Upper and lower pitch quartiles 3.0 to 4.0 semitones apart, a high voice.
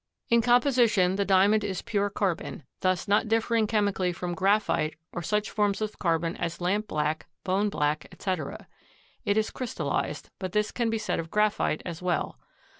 Yes: average, 3.3 semitones; high, 200 Hz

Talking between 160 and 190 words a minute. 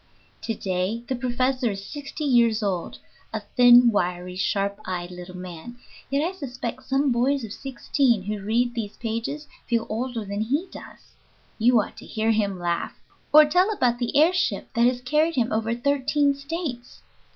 Yes: average, 175 wpm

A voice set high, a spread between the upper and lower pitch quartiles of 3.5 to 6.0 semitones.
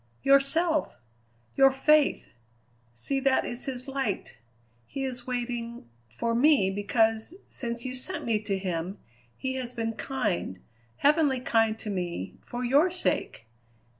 Yes: high, 245 Hz; average, 3.8 semitones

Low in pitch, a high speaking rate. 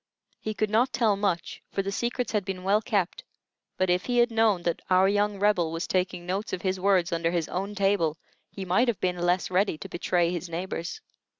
No: high, 190 Hz; fast, 215 wpm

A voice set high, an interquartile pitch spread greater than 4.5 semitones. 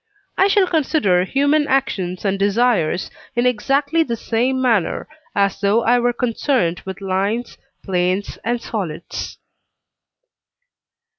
Yes: high, 230 Hz; average, 5.2 semitones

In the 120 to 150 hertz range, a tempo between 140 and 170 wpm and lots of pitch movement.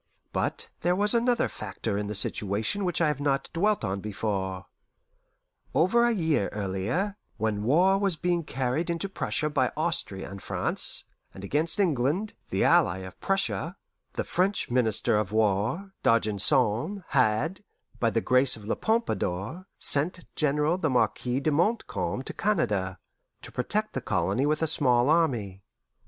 Yes: medium, 140 Hz; average, 150 wpm; wide, 8.8 semitones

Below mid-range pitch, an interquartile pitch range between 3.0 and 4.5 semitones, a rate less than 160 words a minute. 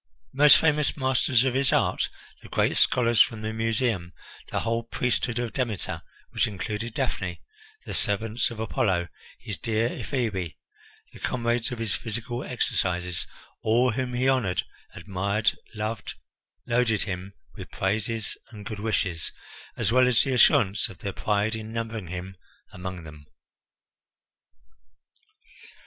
Yes: low, 110 Hz; average, 3.4 semitones; average, 140 wpm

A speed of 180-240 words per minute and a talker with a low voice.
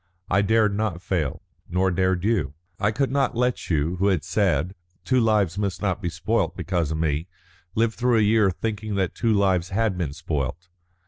Yes: average, 190 wpm; very low, 95 Hz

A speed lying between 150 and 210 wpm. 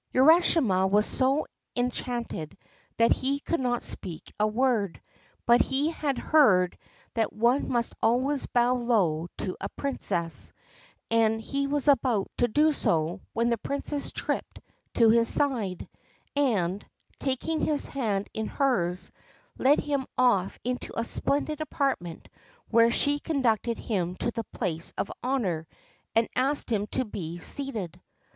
No: average, 140 wpm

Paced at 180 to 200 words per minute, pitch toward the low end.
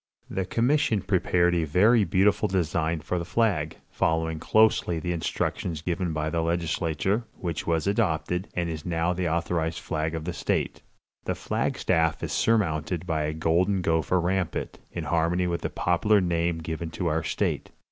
No: average, 170 wpm; very low, 85 Hz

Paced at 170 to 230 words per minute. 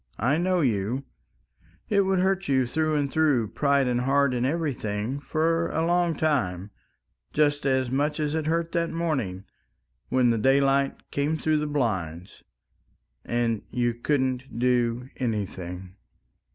No: average, 145 wpm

